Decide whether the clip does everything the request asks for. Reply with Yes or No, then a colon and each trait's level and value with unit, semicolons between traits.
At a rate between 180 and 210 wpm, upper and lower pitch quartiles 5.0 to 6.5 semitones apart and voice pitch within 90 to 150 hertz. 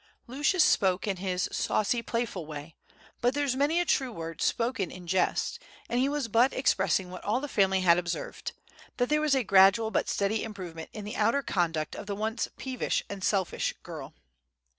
No: average, 185 wpm; wide, 5.5 semitones; high, 210 Hz